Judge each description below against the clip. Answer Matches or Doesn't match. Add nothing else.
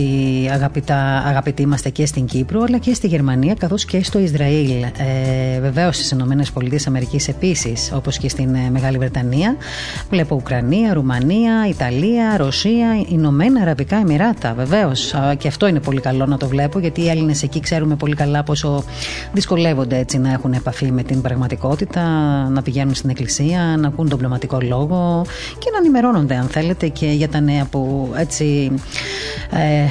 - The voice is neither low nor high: Matches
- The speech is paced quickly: Doesn't match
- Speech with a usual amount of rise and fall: Matches